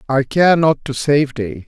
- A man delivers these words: Yes, male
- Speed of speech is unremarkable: No, fast, 215 wpm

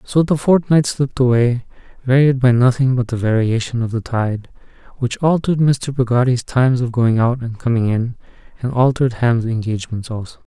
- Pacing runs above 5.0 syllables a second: Yes, 5.4 syllables/s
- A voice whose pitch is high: No, low, 125 Hz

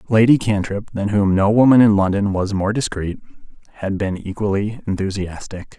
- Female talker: No, male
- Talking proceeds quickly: No, average, 155 wpm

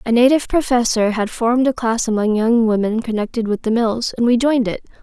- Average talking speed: No, fast, 215 wpm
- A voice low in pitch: No, high, 230 Hz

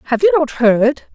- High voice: Yes, very high, 270 Hz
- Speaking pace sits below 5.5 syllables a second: No, 5.7 syllables/s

